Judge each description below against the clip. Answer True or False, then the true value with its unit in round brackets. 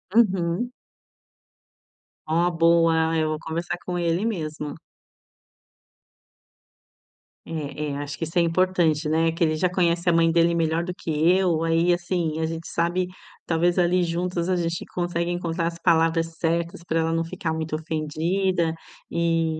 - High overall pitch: False (165 Hz)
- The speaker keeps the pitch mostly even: True (1.3 semitones)